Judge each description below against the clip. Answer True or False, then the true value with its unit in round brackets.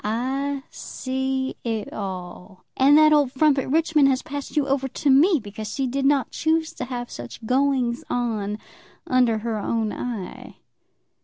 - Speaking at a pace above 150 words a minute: True (160 wpm)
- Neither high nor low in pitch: False (260 Hz)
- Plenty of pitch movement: False (3.8 semitones)